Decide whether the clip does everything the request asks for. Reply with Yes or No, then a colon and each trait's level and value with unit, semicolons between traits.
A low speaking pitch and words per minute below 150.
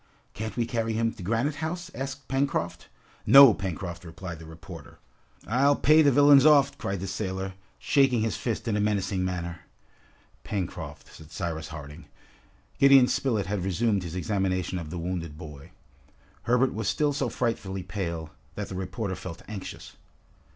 No: low, 100 Hz; average, 160 wpm